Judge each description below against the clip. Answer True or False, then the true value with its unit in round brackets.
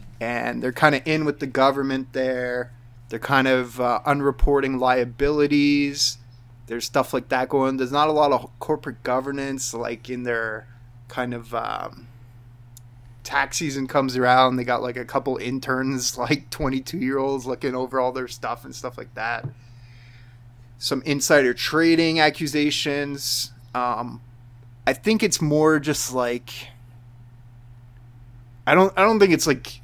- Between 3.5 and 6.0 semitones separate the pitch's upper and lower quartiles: False (2.7 semitones)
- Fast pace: False (150 wpm)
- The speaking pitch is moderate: False (125 Hz)